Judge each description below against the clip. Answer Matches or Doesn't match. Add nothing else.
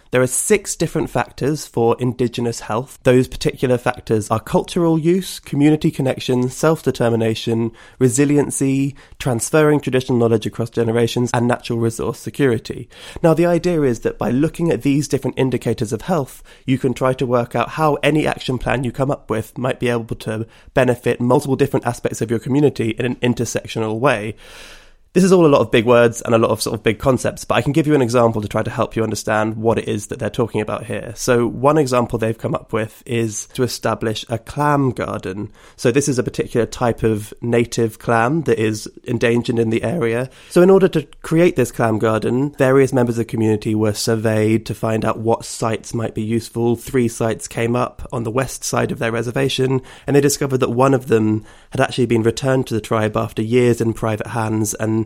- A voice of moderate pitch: Doesn't match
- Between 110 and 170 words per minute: Doesn't match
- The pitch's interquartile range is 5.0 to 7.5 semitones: Doesn't match